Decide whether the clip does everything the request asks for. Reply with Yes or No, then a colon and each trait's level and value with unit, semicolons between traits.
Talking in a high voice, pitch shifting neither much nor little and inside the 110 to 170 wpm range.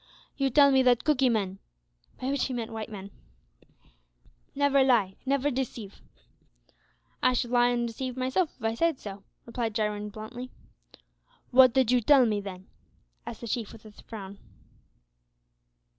Yes: high, 240 Hz; average, 3.4 semitones; average, 155 wpm